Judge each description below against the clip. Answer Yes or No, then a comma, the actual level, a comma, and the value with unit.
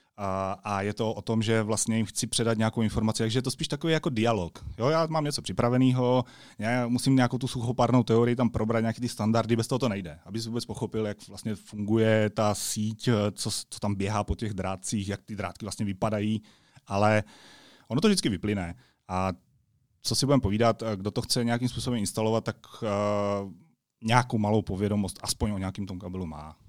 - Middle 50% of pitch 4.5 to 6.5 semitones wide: No, average, 2.8 semitones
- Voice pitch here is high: No, low, 110 Hz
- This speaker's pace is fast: Yes, fast, 195 wpm